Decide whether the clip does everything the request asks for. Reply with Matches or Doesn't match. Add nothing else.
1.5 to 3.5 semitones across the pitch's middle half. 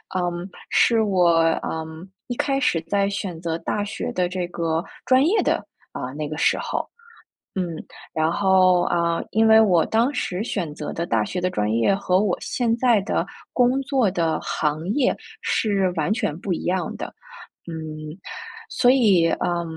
Doesn't match